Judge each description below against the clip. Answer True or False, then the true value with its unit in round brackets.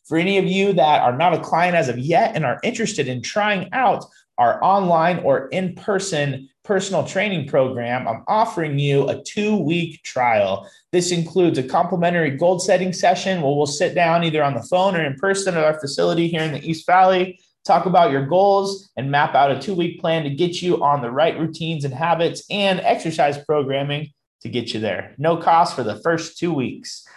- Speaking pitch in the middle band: True (165 Hz)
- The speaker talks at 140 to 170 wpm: False (205 wpm)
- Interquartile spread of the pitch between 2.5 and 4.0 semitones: False (4.4 semitones)